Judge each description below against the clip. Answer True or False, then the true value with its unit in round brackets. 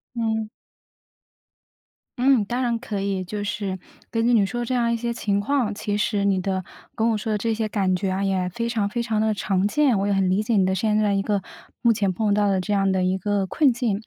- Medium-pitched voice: False (210 Hz)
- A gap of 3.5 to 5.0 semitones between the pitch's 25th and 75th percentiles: False (2.8 semitones)